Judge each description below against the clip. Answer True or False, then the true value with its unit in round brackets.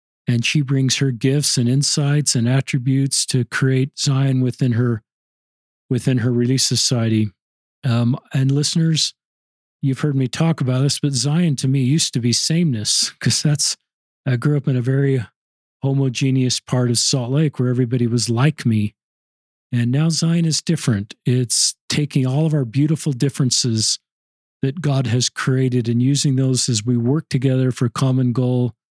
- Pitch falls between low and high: False (130 Hz)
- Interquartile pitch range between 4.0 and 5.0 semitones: False (2.7 semitones)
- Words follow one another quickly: False (165 wpm)